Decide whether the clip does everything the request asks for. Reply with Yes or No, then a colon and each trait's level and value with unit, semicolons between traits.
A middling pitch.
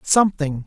Yes: medium, 165 Hz